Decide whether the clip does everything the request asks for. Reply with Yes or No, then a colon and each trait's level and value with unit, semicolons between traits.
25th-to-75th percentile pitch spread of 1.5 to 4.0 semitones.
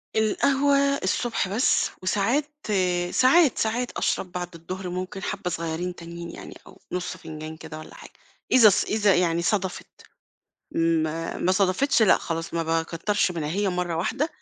No: average, 4.6 semitones